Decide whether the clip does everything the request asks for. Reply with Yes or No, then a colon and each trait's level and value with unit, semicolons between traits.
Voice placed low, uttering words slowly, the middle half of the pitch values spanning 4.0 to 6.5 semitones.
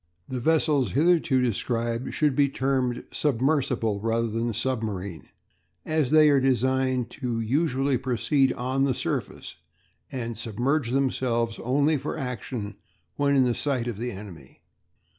No: low, 130 Hz; slow, 130 wpm; average, 3.1 semitones